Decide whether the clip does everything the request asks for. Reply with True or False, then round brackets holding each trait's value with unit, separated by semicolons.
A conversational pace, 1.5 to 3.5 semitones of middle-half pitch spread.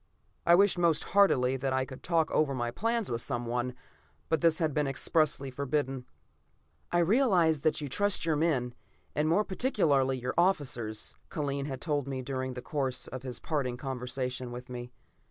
False (175 wpm; 4.3 semitones)